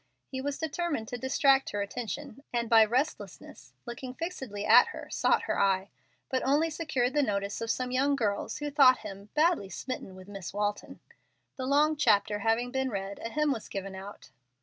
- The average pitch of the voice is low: No, high, 245 Hz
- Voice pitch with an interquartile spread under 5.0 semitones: No, wide, 5.4 semitones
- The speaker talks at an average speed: Yes, average, 190 wpm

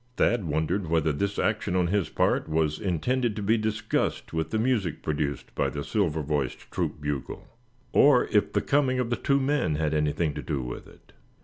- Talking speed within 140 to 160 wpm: No, average, 195 wpm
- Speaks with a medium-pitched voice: No, very low, 85 Hz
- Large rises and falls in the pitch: Yes, wide, 6.7 semitones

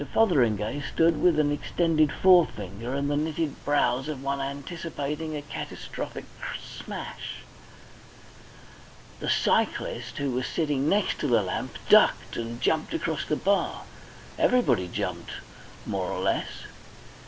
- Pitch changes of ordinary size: Yes, average, 3.4 semitones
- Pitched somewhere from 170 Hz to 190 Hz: No, medium, 145 Hz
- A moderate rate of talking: No, slow, 120 wpm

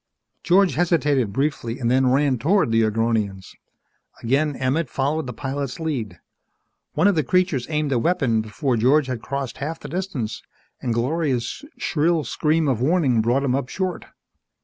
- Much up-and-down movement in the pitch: No, average, 4.9 semitones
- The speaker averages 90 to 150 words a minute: No, average, 160 wpm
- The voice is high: No, low, 135 Hz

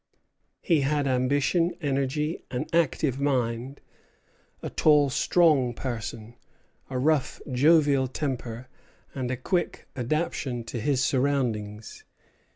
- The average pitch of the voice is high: No, low, 135 Hz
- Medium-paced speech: No, slow, 105 wpm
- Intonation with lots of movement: No, average, 3.1 semitones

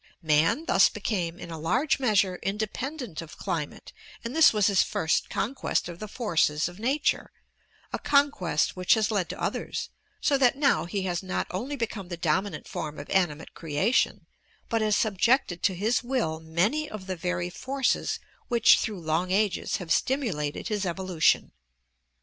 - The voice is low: No, high, 195 Hz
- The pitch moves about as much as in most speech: No, wide, 5.7 semitones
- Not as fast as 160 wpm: No, average, 165 wpm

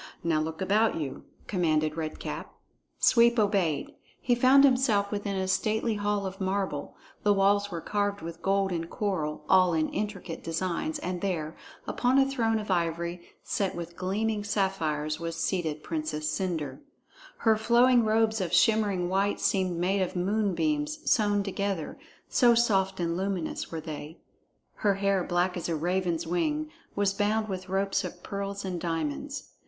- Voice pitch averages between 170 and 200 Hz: Yes, high, 190 Hz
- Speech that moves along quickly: No, average, 160 wpm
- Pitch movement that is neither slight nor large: Yes, average, 3.7 semitones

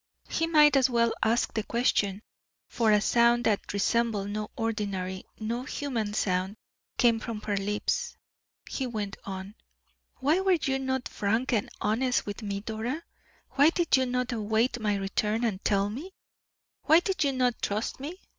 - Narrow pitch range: No, average, 4.0 semitones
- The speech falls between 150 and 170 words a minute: Yes, average, 165 wpm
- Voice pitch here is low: No, high, 230 Hz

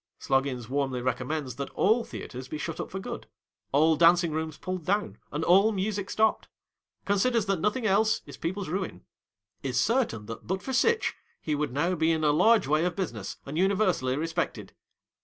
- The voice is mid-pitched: Yes, medium, 165 Hz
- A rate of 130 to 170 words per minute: No, average, 180 wpm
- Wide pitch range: Yes, wide, 6.0 semitones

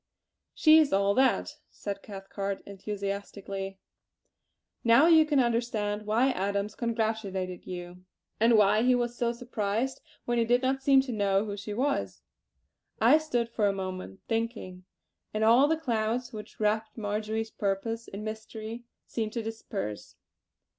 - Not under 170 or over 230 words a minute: No, average, 145 wpm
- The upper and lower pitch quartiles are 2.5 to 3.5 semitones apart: Yes, average, 3.2 semitones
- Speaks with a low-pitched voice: No, high, 220 Hz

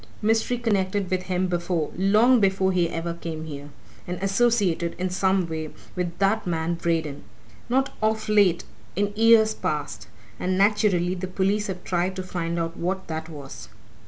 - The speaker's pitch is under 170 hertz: No, medium, 185 Hz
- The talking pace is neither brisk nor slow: Yes, average, 160 wpm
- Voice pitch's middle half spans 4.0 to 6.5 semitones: No, average, 3.2 semitones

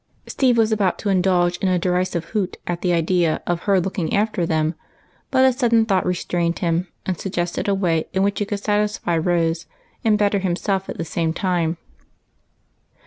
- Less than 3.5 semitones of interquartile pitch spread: Yes, average, 2.9 semitones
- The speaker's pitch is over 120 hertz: Yes, medium, 185 Hz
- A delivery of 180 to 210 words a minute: Yes, average, 185 wpm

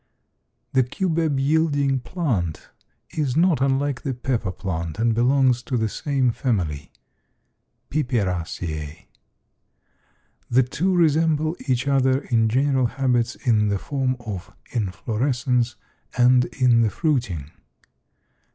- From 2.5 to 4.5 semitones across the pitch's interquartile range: Yes, average, 3.9 semitones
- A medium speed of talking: No, slow, 110 wpm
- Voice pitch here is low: Yes, low, 125 Hz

